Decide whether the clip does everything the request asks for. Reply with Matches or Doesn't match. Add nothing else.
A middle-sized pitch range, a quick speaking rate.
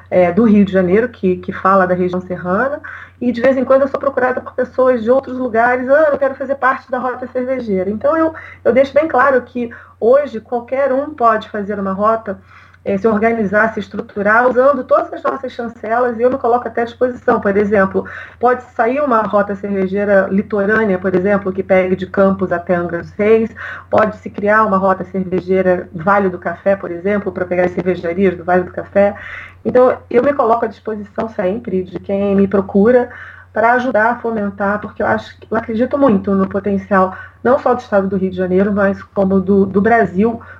Matches